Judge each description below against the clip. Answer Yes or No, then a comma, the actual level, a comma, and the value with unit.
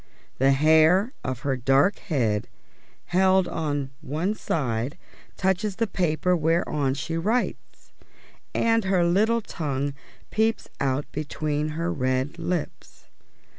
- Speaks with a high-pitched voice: No, medium, 160 Hz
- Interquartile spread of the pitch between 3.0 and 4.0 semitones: No, average, 5.2 semitones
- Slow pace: Yes, slow, 115 wpm